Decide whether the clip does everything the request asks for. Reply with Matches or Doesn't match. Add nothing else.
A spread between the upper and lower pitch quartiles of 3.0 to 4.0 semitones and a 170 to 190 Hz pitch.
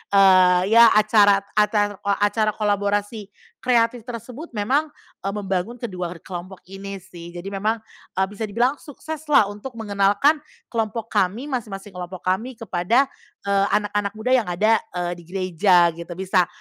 Doesn't match